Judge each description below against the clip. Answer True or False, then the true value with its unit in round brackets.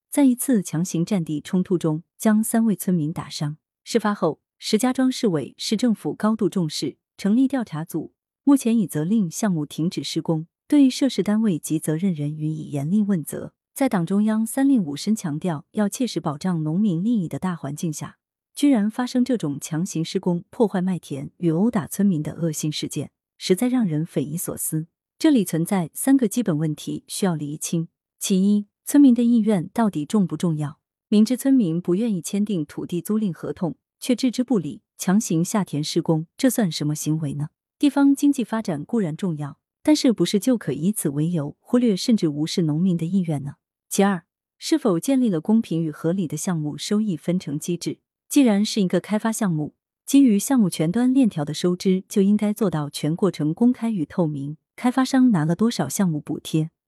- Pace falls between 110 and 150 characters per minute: False (290 characters per minute)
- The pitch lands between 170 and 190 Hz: True (185 Hz)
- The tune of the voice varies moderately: False (6.0 semitones)